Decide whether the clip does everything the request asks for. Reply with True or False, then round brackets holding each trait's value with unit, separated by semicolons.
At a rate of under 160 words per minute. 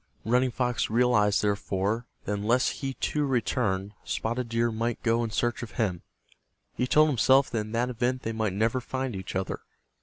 False (180 wpm)